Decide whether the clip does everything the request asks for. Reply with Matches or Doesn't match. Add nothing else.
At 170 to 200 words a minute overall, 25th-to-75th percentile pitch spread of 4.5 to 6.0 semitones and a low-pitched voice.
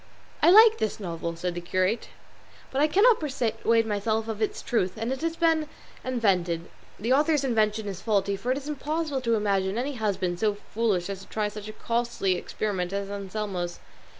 Doesn't match